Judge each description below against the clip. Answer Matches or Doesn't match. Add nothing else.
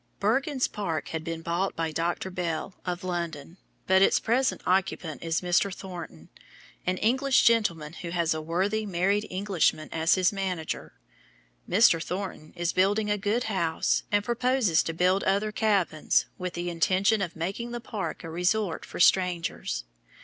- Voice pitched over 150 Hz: Matches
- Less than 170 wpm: Matches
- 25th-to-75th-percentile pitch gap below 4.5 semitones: Matches